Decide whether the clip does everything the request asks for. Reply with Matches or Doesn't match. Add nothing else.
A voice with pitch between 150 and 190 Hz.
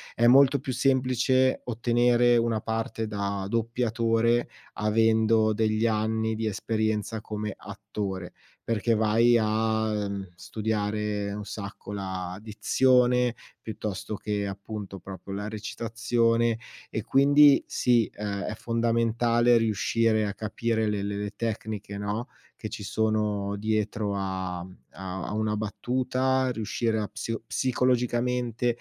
Doesn't match